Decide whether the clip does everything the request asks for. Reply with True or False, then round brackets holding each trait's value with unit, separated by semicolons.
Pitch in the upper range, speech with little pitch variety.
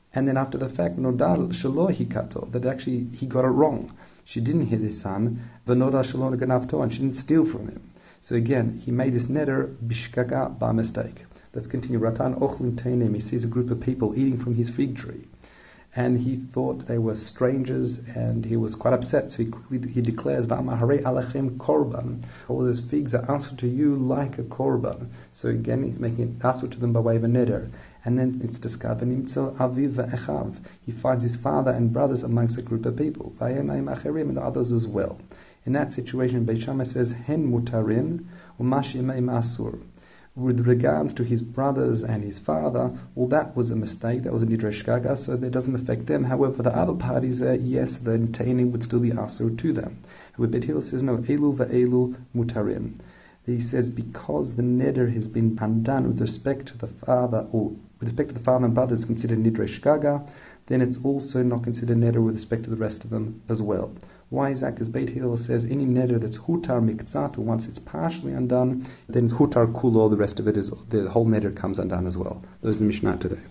False (120 Hz; 2.3 semitones)